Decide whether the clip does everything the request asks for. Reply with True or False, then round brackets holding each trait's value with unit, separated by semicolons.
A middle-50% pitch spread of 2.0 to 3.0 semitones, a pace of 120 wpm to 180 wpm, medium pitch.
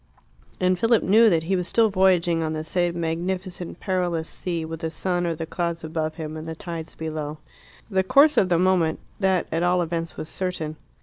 False (2.4 semitones; 200 wpm; 170 Hz)